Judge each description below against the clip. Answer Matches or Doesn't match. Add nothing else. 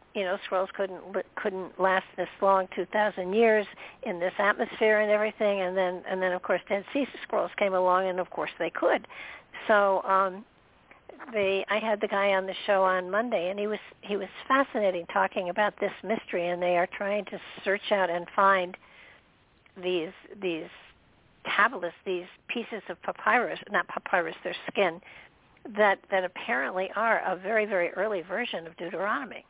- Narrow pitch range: Matches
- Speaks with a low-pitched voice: Doesn't match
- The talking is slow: Doesn't match